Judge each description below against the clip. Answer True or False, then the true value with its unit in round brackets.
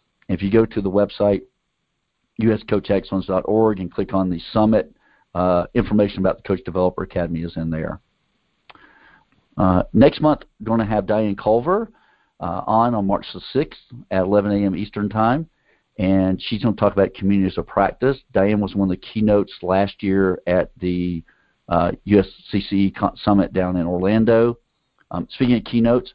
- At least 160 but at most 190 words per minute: True (165 wpm)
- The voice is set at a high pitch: False (100 Hz)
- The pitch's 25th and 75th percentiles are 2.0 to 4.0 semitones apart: True (3.0 semitones)